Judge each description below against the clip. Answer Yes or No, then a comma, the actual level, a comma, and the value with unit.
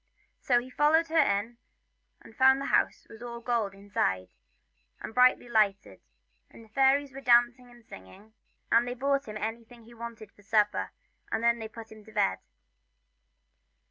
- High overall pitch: Yes, high, 235 Hz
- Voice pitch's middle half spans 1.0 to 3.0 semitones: Yes, narrow, 2.6 semitones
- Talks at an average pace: Yes, average, 175 wpm